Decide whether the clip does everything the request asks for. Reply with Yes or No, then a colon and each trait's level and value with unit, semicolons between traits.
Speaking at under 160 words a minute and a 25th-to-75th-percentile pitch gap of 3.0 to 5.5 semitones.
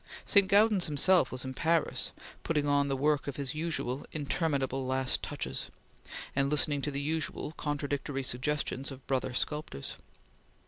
No: average, 140 wpm; narrow, 2.5 semitones